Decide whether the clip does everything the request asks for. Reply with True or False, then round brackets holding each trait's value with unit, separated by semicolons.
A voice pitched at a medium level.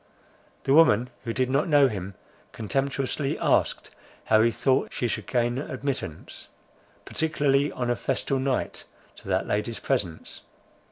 False (130 Hz)